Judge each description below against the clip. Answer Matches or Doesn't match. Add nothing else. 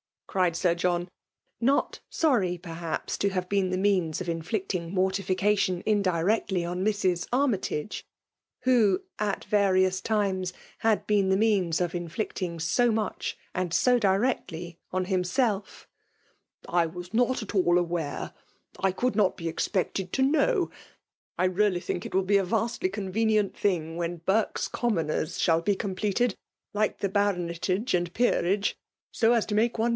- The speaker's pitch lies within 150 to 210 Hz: Matches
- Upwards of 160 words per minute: Doesn't match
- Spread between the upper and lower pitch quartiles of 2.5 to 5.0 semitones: Matches